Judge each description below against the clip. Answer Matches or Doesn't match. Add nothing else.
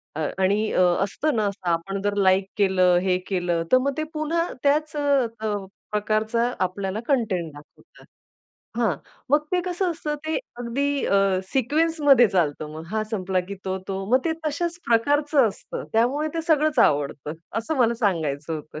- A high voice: Matches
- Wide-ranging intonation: Matches